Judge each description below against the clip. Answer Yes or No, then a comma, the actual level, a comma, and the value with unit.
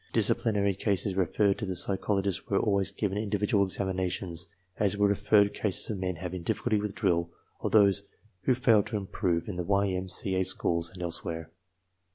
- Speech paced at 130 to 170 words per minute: No, average, 190 wpm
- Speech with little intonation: Yes, narrow, 2.0 semitones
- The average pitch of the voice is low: Yes, very low, 95 Hz